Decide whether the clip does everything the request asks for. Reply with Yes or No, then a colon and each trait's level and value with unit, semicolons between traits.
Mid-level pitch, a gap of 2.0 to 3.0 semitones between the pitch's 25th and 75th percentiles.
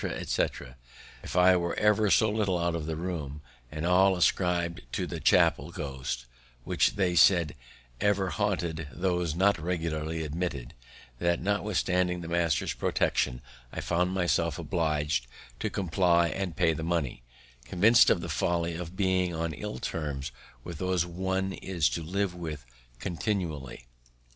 No: very low, 85 Hz; average, 2.7 semitones